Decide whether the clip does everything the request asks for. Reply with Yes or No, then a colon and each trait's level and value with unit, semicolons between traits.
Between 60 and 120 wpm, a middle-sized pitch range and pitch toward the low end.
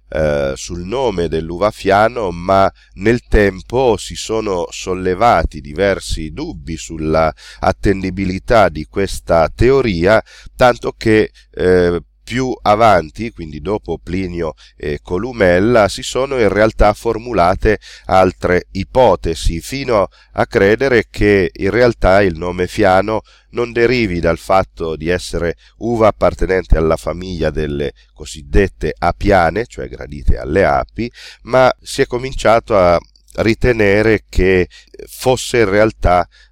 Yes: slow, 115 wpm; average, 4.7 semitones; very low, 95 Hz